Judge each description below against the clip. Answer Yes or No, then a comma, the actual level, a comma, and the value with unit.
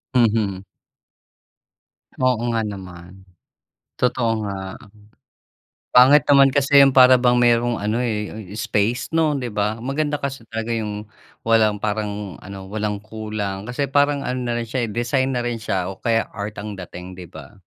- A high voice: No, low, 110 Hz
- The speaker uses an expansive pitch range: No, average, 3.4 semitones